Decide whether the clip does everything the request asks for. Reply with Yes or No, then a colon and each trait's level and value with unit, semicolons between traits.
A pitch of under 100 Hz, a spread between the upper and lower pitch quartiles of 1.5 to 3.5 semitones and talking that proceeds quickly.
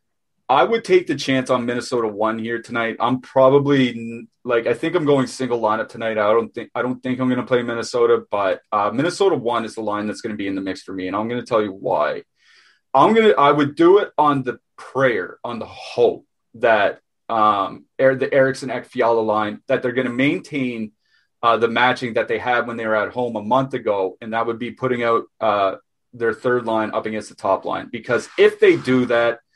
No: low, 120 Hz; narrow, 2.6 semitones; fast, 230 wpm